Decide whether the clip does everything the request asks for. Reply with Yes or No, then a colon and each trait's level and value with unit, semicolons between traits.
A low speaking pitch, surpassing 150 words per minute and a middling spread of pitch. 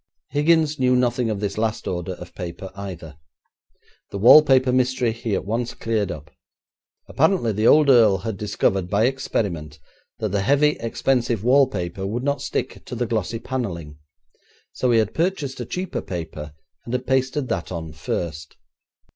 No: low, 115 Hz; average, 160 wpm; wide, 5.8 semitones